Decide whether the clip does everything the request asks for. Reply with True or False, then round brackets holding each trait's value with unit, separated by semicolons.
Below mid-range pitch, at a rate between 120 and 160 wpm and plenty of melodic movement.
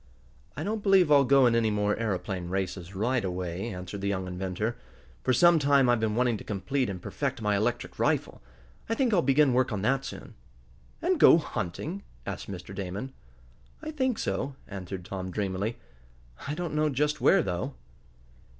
False (110 Hz; 175 wpm; 6.6 semitones)